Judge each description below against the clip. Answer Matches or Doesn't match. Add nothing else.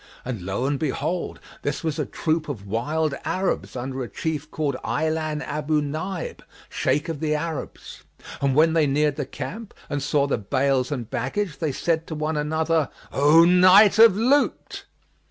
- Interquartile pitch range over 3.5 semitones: Doesn't match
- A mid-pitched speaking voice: Matches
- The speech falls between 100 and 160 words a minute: Doesn't match